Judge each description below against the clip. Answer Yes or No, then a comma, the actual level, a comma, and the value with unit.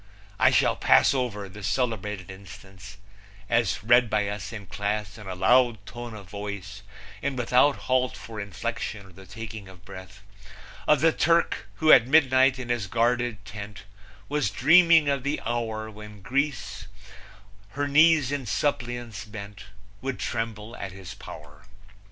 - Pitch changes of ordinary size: Yes, average, 4.3 semitones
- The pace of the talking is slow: No, average, 150 wpm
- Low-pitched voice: Yes, low, 110 Hz